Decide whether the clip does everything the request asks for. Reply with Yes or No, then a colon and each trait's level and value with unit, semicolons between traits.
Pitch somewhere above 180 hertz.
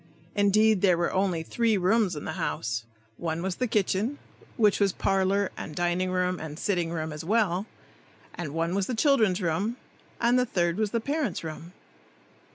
Yes: high, 190 Hz